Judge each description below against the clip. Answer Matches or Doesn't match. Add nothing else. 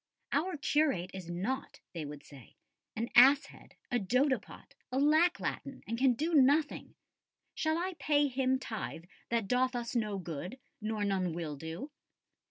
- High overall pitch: Matches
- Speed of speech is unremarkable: Matches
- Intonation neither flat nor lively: Doesn't match